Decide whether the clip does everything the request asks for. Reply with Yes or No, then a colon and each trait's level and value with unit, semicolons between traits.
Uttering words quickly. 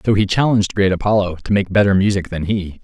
Yes: fast, 235 wpm